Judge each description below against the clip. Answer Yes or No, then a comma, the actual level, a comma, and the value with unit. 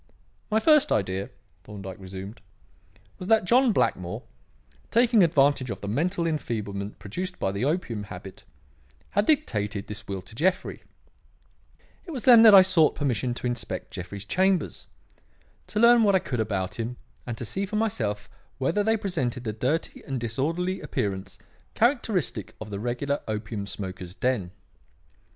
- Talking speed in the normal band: Yes, average, 150 wpm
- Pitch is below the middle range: Yes, low, 125 Hz